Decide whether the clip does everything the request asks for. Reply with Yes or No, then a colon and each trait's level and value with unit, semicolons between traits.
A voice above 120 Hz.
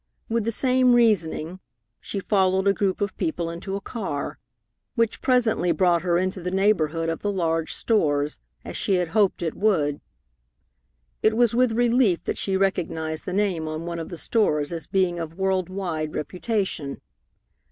Yes: medium, 185 Hz